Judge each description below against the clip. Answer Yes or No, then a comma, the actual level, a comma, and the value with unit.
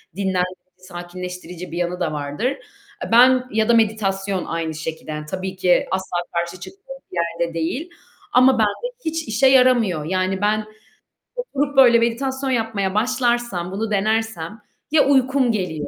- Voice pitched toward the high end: Yes, high, 210 Hz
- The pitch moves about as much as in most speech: No, wide, 5.9 semitones